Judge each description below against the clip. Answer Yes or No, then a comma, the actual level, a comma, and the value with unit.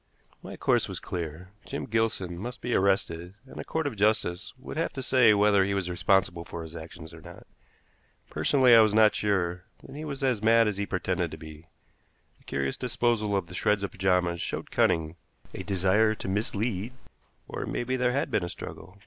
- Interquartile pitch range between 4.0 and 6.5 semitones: Yes, average, 4.5 semitones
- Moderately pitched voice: No, low, 100 Hz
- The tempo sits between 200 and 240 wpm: Yes, fast, 205 wpm